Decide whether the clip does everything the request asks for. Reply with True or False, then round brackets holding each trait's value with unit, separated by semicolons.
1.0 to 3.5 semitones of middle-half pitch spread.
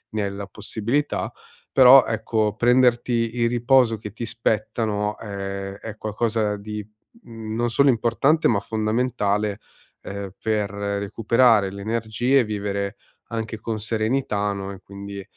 True (2.5 semitones)